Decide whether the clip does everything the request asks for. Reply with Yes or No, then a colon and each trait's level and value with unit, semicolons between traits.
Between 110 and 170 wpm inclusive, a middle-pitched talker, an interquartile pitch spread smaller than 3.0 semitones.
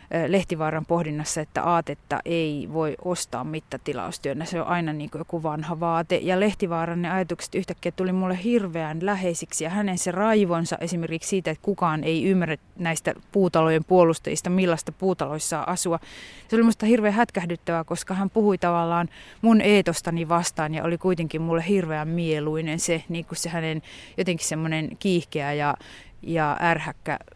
Yes: average, 150 wpm; medium, 170 Hz; narrow, 2.5 semitones